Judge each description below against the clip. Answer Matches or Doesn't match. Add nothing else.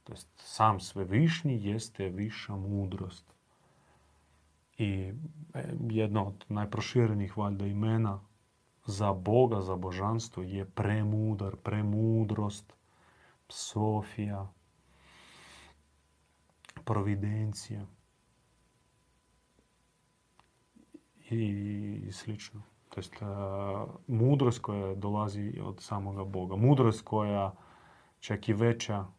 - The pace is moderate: Doesn't match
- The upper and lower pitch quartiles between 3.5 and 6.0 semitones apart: Doesn't match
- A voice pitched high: Doesn't match